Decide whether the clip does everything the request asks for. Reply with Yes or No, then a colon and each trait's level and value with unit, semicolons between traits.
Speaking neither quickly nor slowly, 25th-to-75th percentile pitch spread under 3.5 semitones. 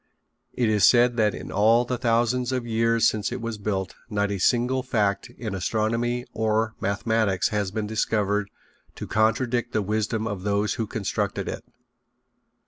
Yes: average, 160 wpm; narrow, 2.4 semitones